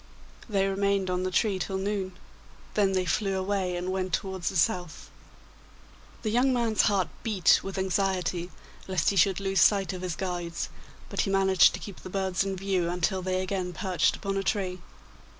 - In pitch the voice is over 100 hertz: Yes, high, 190 Hz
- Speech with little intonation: Yes, narrow, 1.4 semitones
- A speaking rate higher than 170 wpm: Yes, average, 185 wpm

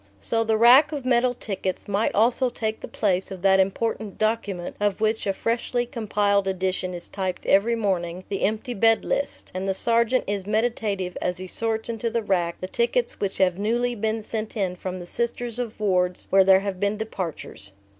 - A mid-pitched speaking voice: No, high, 210 Hz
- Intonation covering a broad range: No, average, 3.3 semitones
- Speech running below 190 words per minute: No, average, 195 wpm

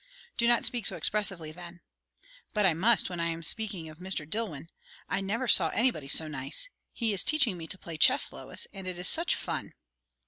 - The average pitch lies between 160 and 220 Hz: Yes, medium, 185 Hz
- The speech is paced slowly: No, fast, 205 wpm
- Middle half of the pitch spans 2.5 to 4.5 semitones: No, average, 5.3 semitones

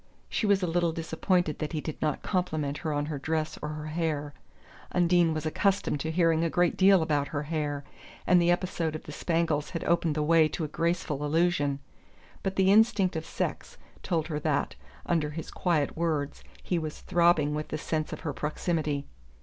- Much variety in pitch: No, narrow, 2.4 semitones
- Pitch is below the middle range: No, medium, 160 Hz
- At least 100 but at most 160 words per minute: No, average, 195 wpm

